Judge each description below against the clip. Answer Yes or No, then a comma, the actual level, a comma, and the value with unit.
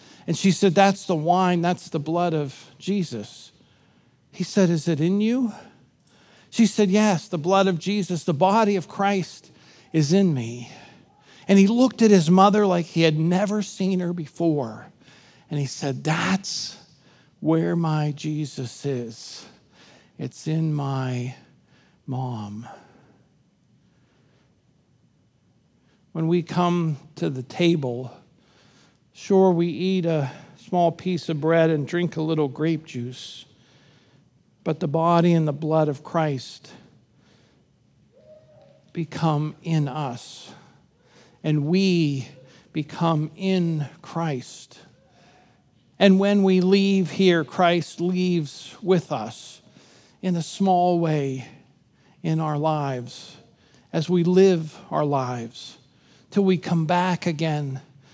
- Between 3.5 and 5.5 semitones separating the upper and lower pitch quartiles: Yes, average, 4.0 semitones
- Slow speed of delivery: Yes, slow, 120 wpm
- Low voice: No, medium, 165 Hz